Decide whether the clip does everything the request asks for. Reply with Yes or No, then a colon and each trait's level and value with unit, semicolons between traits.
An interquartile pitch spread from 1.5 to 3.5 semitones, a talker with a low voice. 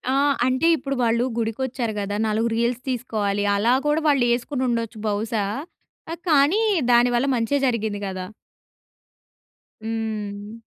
No: average, 2.9 semitones; high, 230 Hz